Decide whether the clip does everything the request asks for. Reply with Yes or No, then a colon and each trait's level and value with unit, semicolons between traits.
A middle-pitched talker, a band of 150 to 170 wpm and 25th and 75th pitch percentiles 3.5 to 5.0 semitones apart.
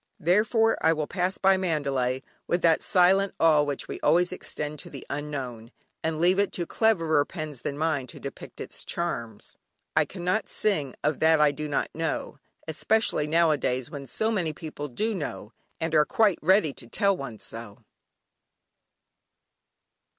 Yes: medium, 160 Hz; average, 160 wpm; average, 4.3 semitones